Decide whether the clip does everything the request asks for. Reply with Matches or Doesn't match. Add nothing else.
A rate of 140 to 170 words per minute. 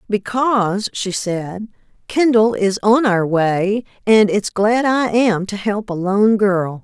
Matches